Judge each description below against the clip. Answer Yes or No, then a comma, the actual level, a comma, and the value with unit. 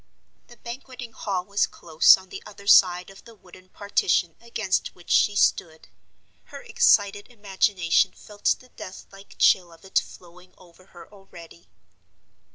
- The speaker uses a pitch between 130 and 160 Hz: No, high, 195 Hz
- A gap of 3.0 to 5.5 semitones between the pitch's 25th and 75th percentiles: No, narrow, 2.5 semitones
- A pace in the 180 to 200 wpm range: No, average, 150 wpm